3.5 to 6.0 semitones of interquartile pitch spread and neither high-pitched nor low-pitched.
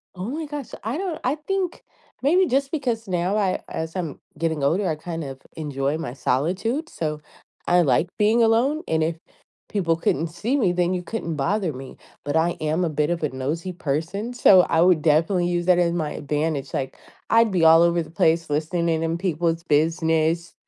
Yes: average, 4.4 semitones; medium, 170 Hz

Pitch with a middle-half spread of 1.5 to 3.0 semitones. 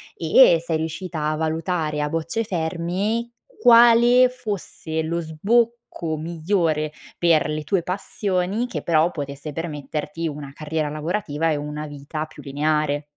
No: average, 3.6 semitones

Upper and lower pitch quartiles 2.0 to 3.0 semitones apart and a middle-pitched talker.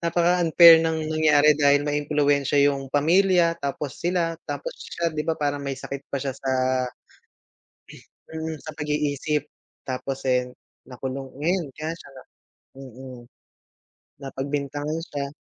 Yes: average, 2.7 semitones; medium, 145 Hz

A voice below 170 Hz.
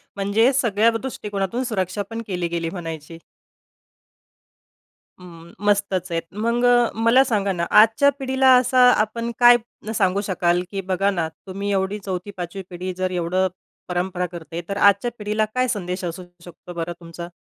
No: high, 195 Hz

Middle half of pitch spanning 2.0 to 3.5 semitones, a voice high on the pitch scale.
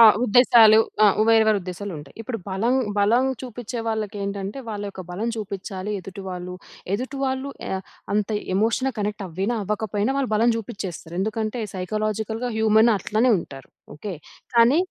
Yes: average, 2.9 semitones; high, 215 Hz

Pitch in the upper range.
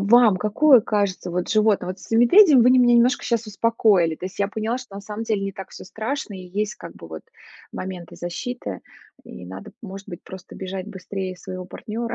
Yes: high, 200 Hz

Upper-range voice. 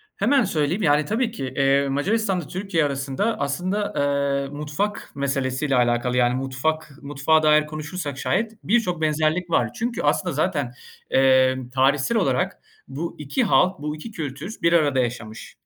No: medium, 150 Hz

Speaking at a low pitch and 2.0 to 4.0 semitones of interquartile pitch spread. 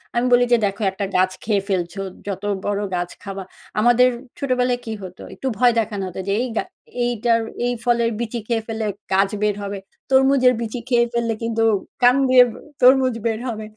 No: high, 230 Hz; average, 3.5 semitones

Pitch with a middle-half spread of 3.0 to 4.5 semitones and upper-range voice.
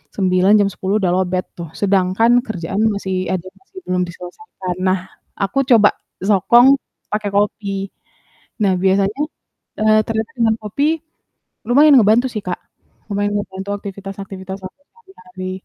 No: narrow, 2.5 semitones; high, 200 Hz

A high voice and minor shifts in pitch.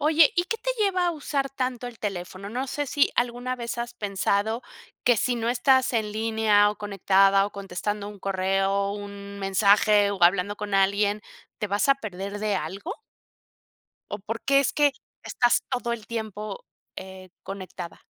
No: high, 210 Hz; average, 3.7 semitones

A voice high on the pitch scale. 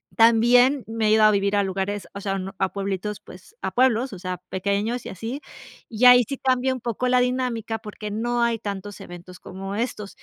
Yes: high, 220 Hz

